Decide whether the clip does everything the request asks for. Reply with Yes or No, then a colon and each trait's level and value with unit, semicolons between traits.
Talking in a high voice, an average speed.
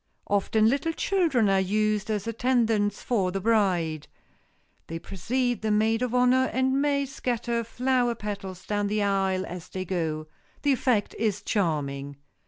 Yes: high, 215 Hz; average, 150 wpm